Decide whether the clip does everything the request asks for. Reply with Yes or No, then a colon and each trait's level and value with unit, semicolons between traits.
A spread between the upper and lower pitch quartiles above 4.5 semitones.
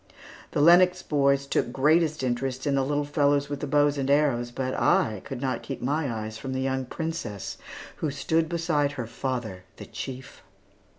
No: narrow, 2.4 semitones